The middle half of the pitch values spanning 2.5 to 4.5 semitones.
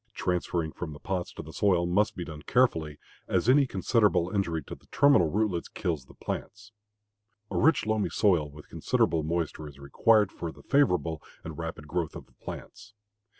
No: average, 4.9 semitones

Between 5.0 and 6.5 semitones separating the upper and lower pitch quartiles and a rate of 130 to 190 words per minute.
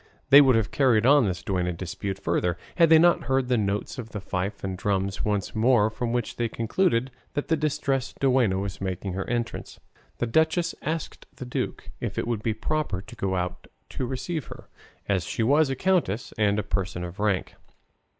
No: wide, 5.5 semitones; average, 200 wpm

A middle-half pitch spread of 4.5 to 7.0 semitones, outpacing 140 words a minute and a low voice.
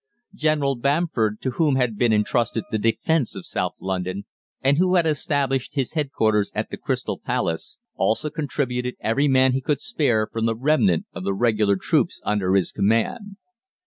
Yes: average, 5.3 semitones; average, 170 wpm; low, 125 Hz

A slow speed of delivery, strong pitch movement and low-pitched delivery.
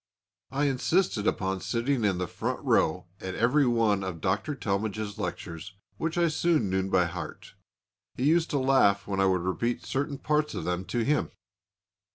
No: average, 175 wpm; wide, 6.8 semitones; low, 110 Hz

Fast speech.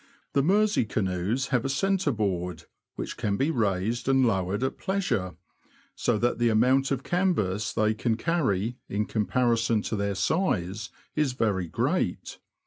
No: average, 150 wpm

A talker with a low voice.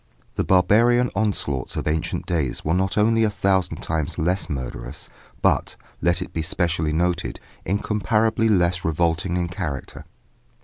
Yes: very low, 90 Hz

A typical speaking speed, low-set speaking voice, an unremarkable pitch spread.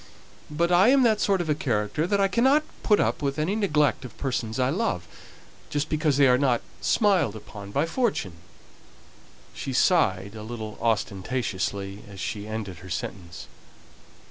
No: average, 165 wpm; low, 130 Hz; wide, 9.0 semitones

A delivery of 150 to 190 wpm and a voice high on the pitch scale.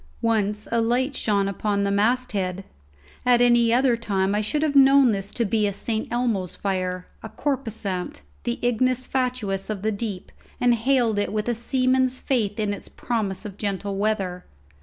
Yes: average, 175 wpm; high, 220 Hz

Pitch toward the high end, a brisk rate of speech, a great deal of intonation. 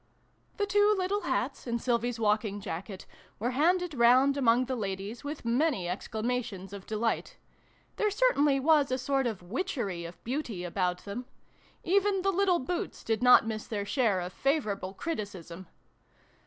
No: high, 240 Hz; average, 155 wpm; wide, 6.8 semitones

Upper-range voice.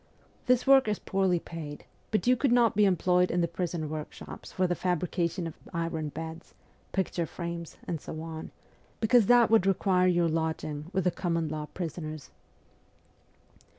No: medium, 175 Hz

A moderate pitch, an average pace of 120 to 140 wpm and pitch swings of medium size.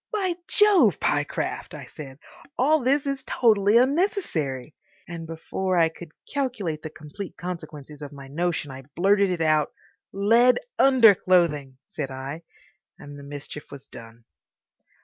No: medium, 170 Hz; slow, 135 wpm; wide, 8.1 semitones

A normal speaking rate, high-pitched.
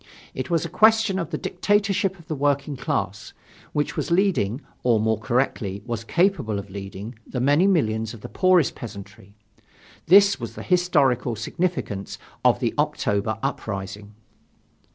No: average, 150 wpm; low, 135 Hz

